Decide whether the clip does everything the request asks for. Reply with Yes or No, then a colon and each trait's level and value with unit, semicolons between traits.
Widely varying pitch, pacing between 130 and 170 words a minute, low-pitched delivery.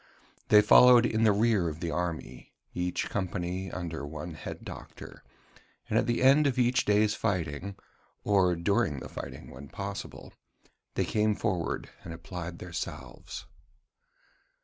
No: average, 4.2 semitones; average, 145 wpm; very low, 95 Hz